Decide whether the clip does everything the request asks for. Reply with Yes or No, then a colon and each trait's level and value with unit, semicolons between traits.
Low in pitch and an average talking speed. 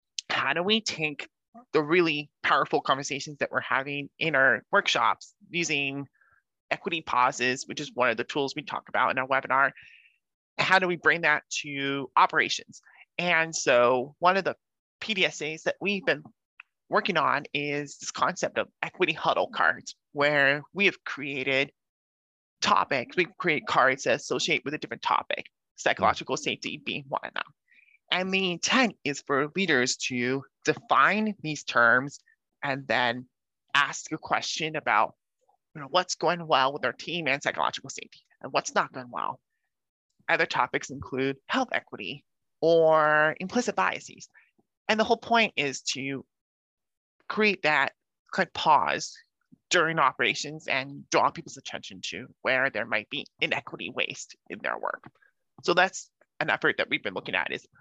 No: medium, 150 Hz; average, 160 wpm